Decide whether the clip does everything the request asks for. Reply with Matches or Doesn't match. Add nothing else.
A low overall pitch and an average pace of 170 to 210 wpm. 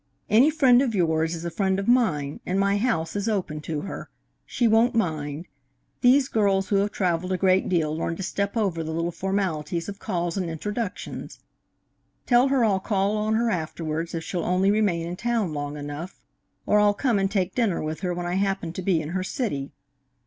Doesn't match